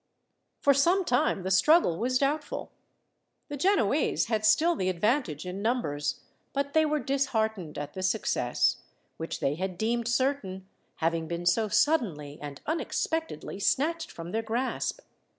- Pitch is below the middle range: No, high, 220 Hz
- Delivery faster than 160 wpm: No, average, 145 wpm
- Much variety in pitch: Yes, wide, 7.7 semitones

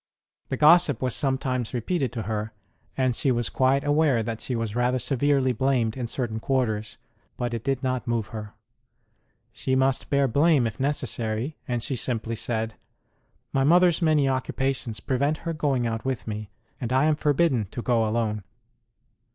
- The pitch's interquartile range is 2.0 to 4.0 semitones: Yes, average, 3.3 semitones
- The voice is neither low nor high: No, low, 130 Hz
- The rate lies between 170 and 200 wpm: Yes, average, 175 wpm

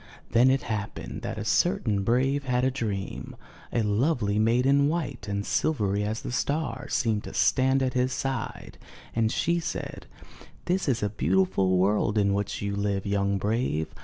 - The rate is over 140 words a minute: Yes, average, 165 wpm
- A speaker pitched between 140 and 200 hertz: No, low, 115 Hz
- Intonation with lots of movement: No, average, 4.7 semitones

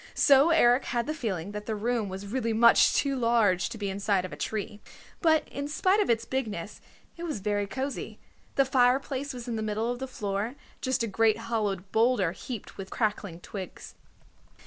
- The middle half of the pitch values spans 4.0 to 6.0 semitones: Yes, average, 4.3 semitones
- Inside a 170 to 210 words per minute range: Yes, average, 190 wpm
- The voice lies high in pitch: Yes, high, 230 Hz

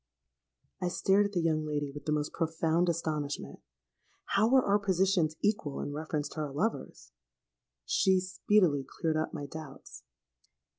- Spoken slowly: No, average, 150 wpm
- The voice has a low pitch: No, medium, 160 Hz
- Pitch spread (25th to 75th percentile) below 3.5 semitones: No, average, 4.0 semitones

